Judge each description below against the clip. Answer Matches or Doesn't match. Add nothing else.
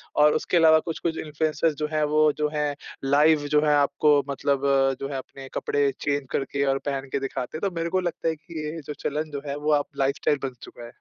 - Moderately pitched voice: Matches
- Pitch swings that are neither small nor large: Doesn't match